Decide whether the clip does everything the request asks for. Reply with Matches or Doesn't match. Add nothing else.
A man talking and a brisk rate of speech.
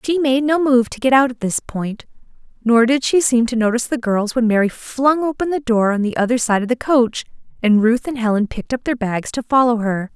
Doesn't match